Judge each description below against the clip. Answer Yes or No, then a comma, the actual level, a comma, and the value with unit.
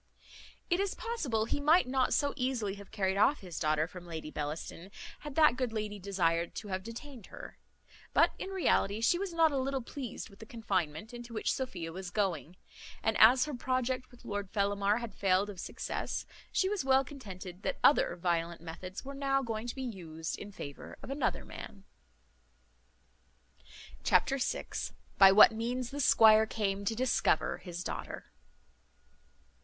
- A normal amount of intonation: No, wide, 5.8 semitones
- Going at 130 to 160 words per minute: No, average, 170 wpm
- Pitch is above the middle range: Yes, high, 220 Hz